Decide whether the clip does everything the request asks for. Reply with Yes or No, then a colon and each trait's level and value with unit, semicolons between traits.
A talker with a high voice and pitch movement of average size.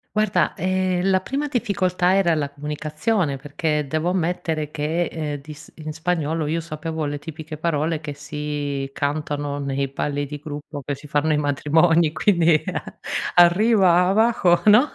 No: medium, 155 Hz; average, 3.3 semitones